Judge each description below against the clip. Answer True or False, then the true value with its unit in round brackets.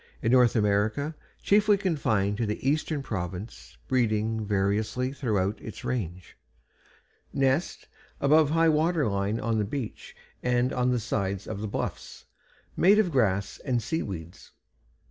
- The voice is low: True (115 Hz)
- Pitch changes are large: True (5.7 semitones)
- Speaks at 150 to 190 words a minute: False (140 wpm)